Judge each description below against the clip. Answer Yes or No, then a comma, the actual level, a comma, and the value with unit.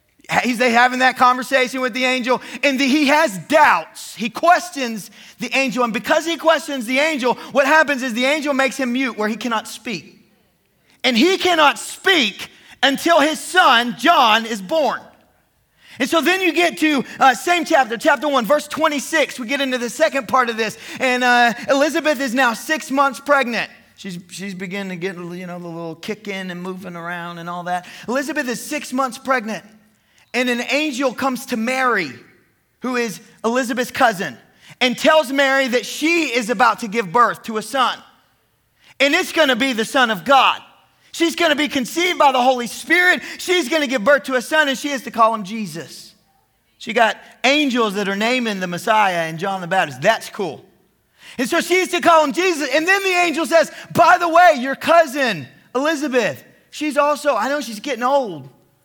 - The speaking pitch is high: Yes, very high, 260 Hz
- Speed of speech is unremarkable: Yes, average, 190 wpm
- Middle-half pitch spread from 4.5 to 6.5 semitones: Yes, average, 4.8 semitones